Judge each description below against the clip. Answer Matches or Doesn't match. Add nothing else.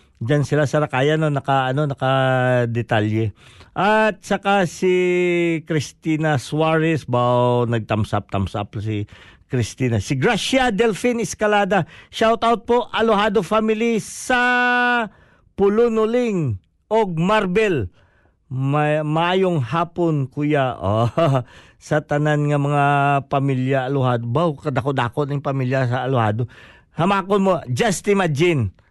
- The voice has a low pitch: Doesn't match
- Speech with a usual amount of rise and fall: Doesn't match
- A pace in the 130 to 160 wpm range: Doesn't match